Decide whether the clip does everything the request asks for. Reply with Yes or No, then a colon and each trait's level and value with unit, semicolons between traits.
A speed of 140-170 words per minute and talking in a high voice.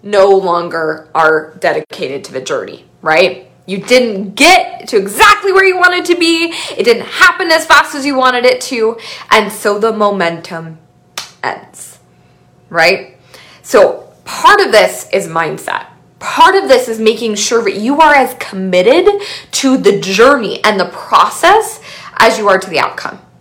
Yes: average, 160 wpm; very high, 250 Hz